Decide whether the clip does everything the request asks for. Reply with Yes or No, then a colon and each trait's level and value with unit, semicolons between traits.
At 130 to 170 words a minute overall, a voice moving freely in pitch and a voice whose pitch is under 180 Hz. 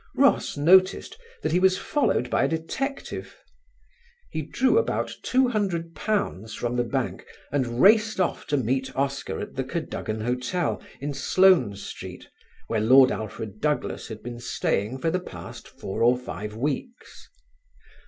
Yes: average, 145 wpm; wide, 7.4 semitones; medium, 140 Hz